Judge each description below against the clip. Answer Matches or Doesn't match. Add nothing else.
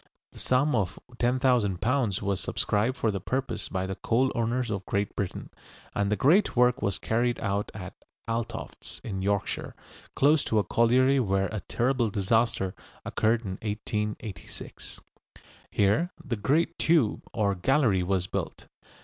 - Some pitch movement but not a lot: Matches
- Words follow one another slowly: Doesn't match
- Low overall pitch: Matches